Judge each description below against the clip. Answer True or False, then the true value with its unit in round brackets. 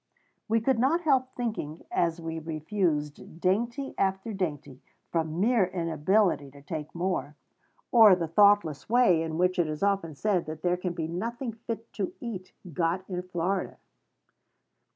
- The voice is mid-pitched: True (180 Hz)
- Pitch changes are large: False (4.9 semitones)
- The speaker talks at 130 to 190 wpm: True (150 wpm)